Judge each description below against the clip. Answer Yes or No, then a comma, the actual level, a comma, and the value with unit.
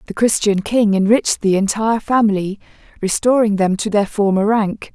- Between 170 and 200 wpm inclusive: No, average, 160 wpm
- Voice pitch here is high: Yes, high, 210 Hz